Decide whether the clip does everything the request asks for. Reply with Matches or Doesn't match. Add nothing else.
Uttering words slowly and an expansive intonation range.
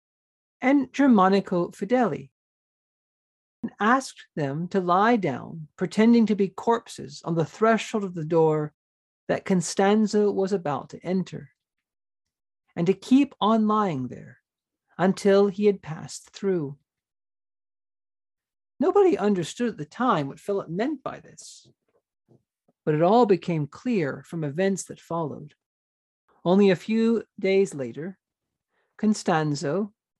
Matches